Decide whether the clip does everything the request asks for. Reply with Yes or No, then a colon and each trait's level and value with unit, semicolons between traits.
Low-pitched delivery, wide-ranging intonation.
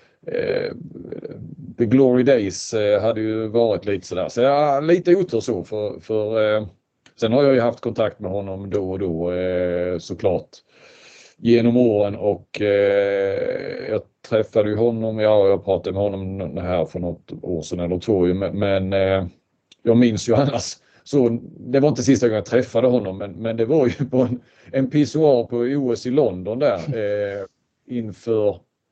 Yes: low, 115 Hz; wide, 5.7 semitones